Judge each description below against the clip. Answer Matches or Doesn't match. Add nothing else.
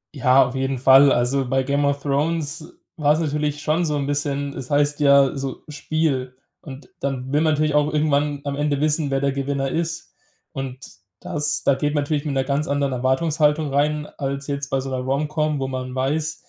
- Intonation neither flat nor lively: Doesn't match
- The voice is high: Doesn't match